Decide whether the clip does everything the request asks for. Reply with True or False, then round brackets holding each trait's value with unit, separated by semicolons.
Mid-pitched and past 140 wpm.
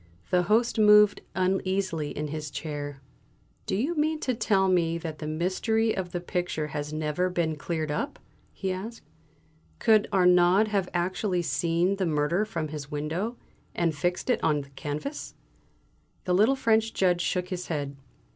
True (180 Hz; 160 wpm)